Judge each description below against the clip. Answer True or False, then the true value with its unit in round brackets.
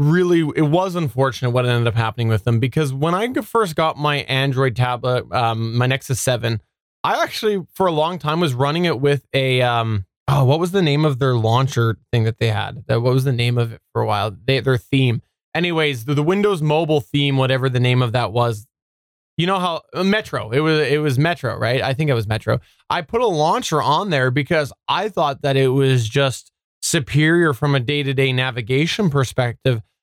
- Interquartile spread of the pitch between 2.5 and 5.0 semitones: True (3.9 semitones)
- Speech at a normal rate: False (210 wpm)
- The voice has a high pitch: False (135 Hz)